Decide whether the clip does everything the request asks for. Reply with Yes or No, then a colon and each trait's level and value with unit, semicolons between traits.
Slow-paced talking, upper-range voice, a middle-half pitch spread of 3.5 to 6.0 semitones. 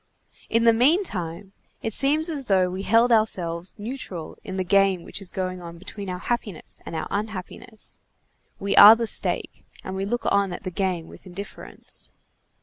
No: average, 175 wpm; high, 195 Hz; average, 3.8 semitones